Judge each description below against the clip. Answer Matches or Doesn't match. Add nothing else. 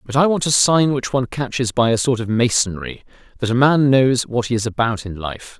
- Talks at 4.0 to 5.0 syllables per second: Doesn't match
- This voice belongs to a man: Matches